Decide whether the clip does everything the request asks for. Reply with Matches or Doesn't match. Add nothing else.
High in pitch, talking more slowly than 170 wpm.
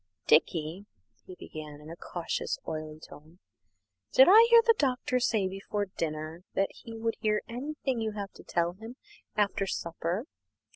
Matches